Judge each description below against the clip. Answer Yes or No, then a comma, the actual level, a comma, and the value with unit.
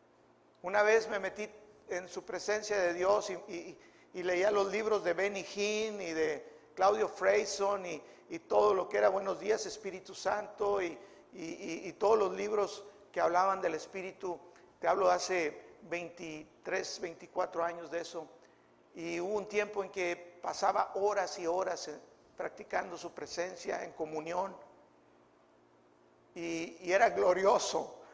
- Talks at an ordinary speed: Yes, average, 150 wpm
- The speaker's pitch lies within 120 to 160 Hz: No, medium, 185 Hz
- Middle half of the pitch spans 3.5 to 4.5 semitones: No, average, 3.1 semitones